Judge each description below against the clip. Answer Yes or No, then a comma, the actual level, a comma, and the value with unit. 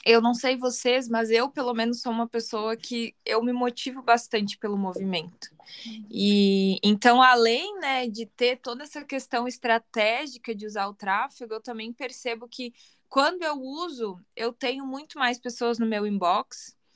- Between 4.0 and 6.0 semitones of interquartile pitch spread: No, narrow, 2.4 semitones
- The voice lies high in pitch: Yes, high, 235 Hz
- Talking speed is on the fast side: No, average, 165 wpm